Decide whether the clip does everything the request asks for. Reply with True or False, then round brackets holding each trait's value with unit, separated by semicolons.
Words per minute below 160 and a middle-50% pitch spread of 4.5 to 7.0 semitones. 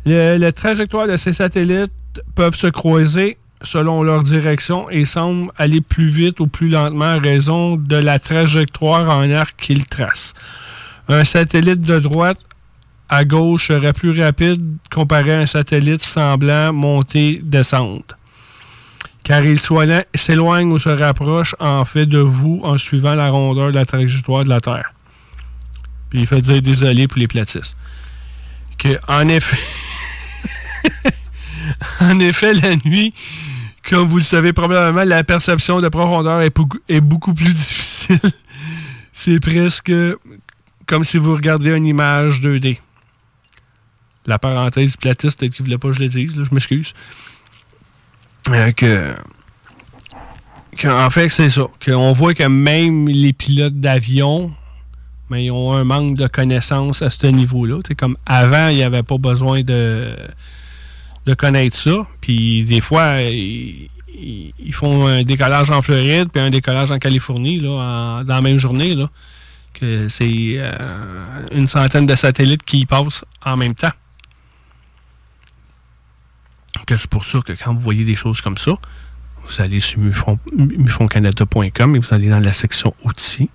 True (150 wpm; 4.9 semitones)